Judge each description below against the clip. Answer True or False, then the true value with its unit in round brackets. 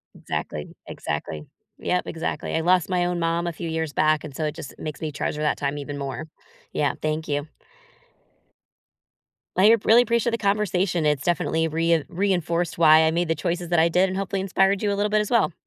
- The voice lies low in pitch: False (170 Hz)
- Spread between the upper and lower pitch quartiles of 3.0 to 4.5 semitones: True (3.5 semitones)